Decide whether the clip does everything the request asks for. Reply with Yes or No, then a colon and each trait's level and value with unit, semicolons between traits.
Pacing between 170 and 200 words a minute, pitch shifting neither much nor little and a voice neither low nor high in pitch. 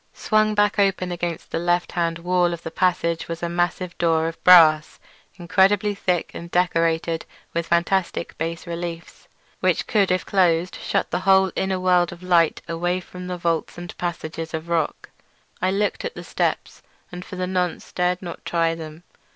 No: average, 175 wpm; narrow, 1.6 semitones; medium, 175 Hz